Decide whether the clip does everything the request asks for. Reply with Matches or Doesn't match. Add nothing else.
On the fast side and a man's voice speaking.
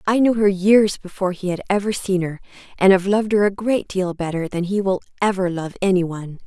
Doesn't match